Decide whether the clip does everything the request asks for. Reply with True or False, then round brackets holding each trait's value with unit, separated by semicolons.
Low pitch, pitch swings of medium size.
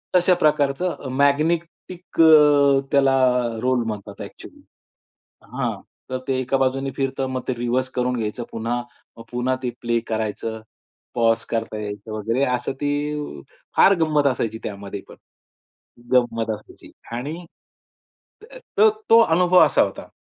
True (130 Hz; 4.0 semitones)